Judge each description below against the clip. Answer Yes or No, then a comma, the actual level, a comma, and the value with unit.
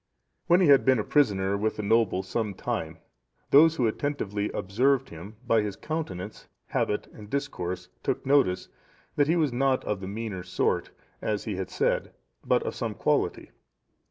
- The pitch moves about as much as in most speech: No, wide, 6.1 semitones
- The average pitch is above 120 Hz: No, low, 110 Hz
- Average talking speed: Yes, average, 170 wpm